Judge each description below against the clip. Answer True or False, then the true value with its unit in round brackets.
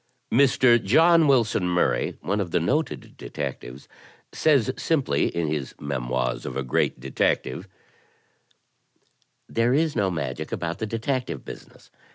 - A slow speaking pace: True (130 wpm)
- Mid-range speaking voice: False (100 Hz)